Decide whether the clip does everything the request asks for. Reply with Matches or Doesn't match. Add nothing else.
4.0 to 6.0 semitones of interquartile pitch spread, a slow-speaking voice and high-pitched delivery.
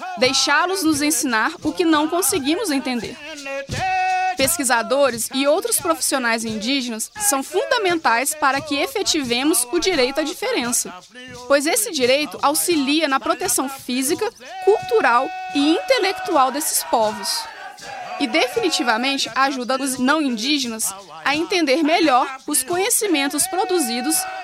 Matches